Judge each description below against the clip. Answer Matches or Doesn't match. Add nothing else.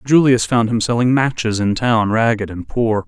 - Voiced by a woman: Doesn't match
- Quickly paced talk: Doesn't match